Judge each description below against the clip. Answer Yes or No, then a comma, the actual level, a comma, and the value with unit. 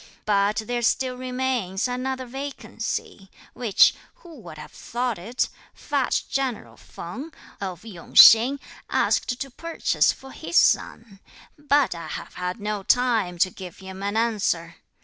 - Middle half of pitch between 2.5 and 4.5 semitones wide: No, average, 5.1 semitones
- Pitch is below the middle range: No, high, 235 Hz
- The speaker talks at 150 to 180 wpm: No, average, 140 wpm